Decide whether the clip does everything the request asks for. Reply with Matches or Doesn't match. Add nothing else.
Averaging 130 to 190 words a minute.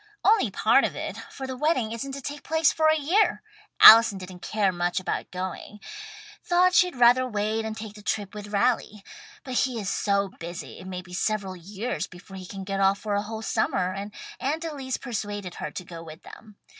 Doesn't match